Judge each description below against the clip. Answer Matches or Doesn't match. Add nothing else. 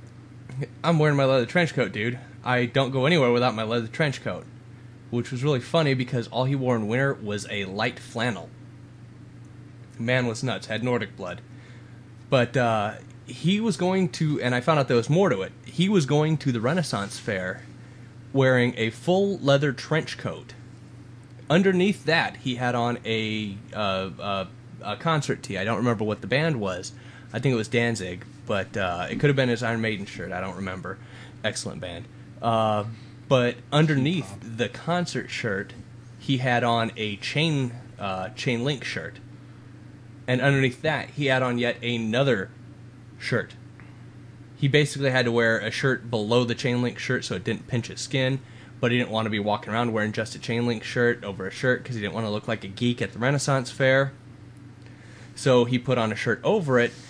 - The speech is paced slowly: Doesn't match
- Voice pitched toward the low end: Matches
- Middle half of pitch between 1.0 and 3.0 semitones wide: Matches